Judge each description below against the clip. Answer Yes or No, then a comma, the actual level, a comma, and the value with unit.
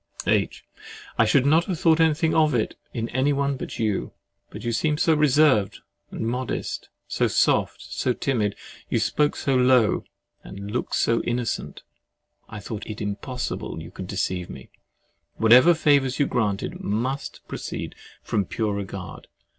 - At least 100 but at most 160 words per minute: Yes, average, 145 wpm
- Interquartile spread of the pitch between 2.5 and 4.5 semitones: No, average, 5.0 semitones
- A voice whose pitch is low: Yes, low, 125 Hz